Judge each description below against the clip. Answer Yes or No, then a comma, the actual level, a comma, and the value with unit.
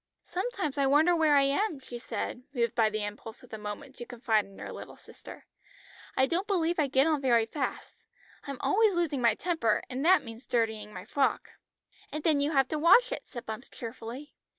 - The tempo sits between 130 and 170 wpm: No, fast, 205 wpm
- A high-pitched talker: Yes, very high, 270 Hz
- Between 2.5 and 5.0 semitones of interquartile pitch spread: No, wide, 5.5 semitones